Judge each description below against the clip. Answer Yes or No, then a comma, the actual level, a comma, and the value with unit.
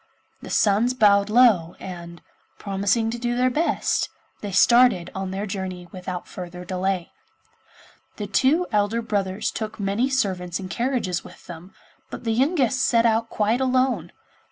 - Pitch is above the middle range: Yes, high, 210 Hz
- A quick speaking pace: No, average, 150 wpm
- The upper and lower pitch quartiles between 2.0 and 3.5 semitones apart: No, average, 4.4 semitones